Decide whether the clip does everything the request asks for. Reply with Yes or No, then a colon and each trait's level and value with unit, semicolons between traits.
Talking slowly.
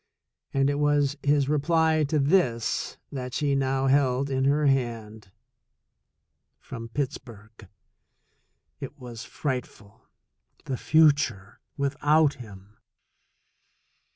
Yes: slow, 100 wpm